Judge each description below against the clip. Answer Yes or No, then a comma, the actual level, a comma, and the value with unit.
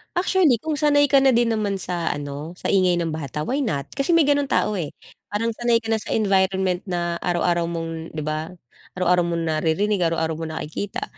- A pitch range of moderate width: No, wide, 5.9 semitones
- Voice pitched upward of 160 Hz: Yes, medium, 185 Hz